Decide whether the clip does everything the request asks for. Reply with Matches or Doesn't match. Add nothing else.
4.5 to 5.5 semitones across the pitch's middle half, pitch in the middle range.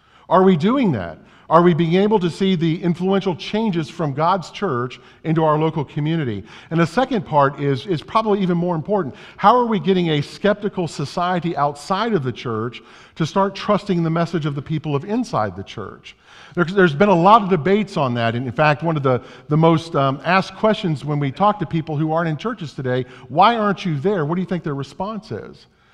Matches